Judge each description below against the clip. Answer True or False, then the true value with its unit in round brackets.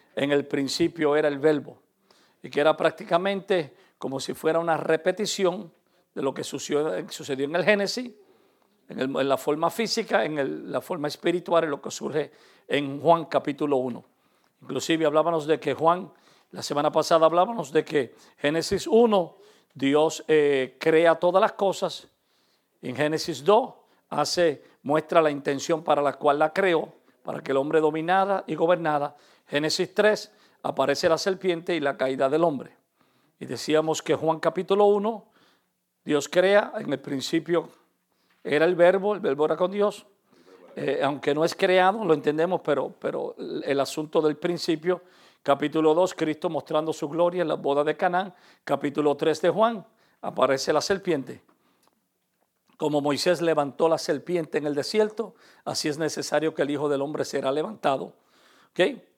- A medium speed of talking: True (160 wpm)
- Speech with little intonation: False (3.7 semitones)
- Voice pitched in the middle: True (160 Hz)